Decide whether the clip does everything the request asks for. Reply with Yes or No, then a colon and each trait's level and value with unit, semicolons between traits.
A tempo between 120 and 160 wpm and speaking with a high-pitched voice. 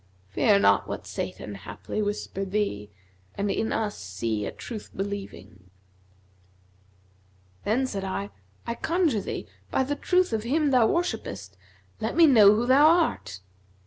Yes: average, 150 wpm; high, 210 Hz